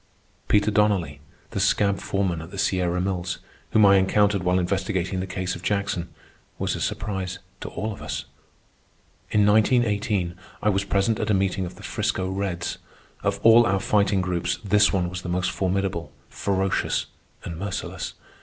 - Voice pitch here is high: No, very low, 95 Hz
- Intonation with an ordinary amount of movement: No, narrow, 2.1 semitones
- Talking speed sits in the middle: Yes, average, 165 wpm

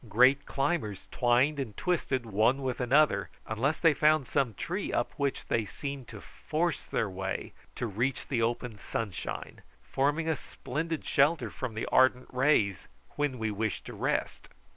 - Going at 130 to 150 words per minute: No, average, 160 wpm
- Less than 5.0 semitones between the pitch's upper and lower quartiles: Yes, average, 4.6 semitones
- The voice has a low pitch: Yes, low, 130 Hz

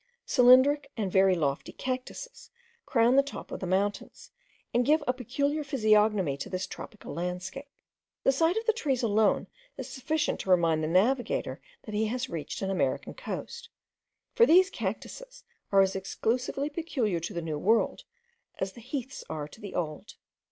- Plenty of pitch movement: Yes, wide, 6.9 semitones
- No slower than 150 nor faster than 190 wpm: Yes, average, 165 wpm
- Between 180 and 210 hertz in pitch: No, high, 230 Hz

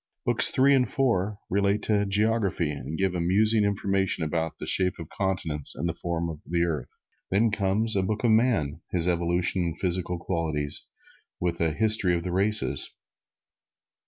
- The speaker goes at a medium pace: Yes, average, 170 wpm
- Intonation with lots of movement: No, average, 3.6 semitones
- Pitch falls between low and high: No, very low, 90 Hz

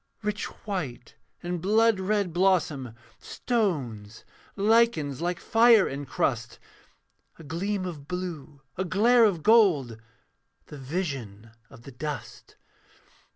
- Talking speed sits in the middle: No, slow, 110 wpm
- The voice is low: No, medium, 175 Hz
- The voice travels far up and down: Yes, wide, 6.8 semitones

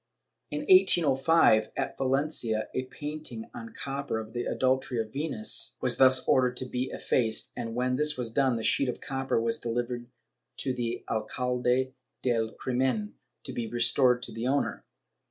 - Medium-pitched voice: No, low, 130 Hz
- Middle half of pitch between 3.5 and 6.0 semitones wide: No, narrow, 2.6 semitones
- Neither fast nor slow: Yes, average, 160 wpm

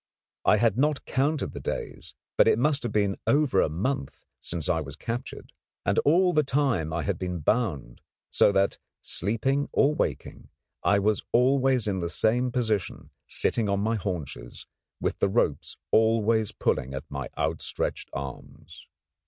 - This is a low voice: Yes, low, 110 Hz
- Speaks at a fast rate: No, average, 160 wpm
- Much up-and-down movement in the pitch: Yes, wide, 6.9 semitones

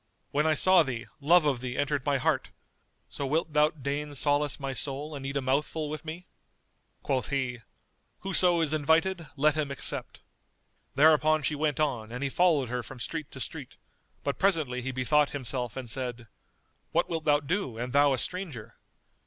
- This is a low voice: No, medium, 145 Hz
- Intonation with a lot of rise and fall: No, average, 3.1 semitones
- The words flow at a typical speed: Yes, average, 180 wpm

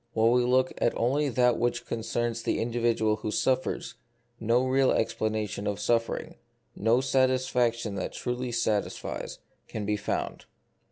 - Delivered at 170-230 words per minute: No, average, 150 wpm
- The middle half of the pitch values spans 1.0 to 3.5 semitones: Yes, narrow, 2.4 semitones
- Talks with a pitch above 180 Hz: No, low, 115 Hz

